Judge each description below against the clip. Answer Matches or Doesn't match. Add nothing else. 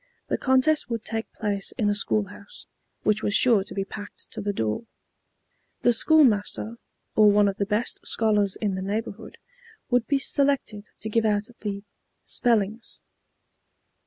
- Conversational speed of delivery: Matches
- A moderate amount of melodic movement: Doesn't match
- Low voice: Doesn't match